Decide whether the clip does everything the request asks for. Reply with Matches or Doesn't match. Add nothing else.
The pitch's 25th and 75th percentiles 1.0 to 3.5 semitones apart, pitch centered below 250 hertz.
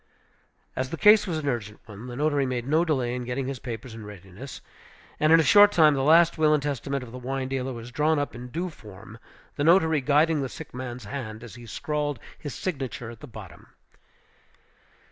Doesn't match